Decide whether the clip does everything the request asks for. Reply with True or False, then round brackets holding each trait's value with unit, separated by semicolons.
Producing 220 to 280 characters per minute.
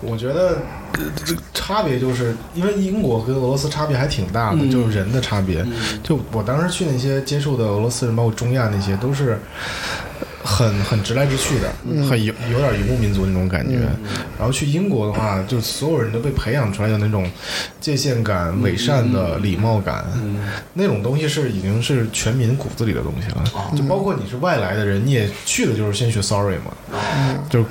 False (300 characters per minute)